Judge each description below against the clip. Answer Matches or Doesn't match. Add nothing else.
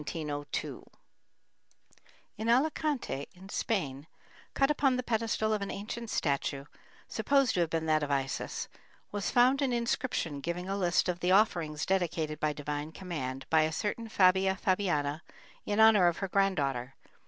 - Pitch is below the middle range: Doesn't match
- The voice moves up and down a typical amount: Doesn't match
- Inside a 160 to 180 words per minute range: Doesn't match